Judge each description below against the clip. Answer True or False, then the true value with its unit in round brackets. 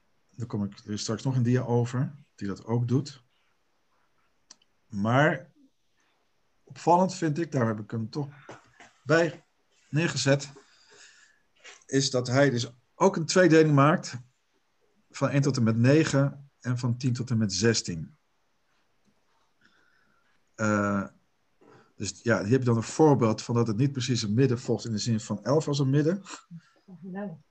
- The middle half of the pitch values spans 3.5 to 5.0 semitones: True (4.5 semitones)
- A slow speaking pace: False (155 wpm)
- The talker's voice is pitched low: True (130 Hz)